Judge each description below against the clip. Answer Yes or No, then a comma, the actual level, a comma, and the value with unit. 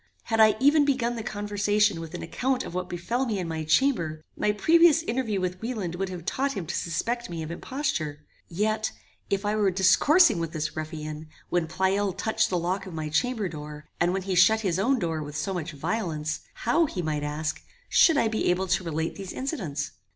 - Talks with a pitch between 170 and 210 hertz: Yes, high, 190 Hz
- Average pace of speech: No, fast, 210 wpm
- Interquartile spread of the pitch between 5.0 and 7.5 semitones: Yes, wide, 5.5 semitones